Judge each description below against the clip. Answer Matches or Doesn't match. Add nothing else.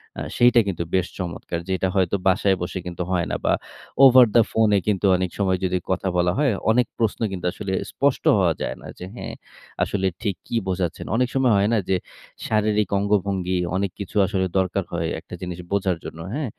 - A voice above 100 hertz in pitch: Doesn't match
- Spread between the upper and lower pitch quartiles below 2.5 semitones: Doesn't match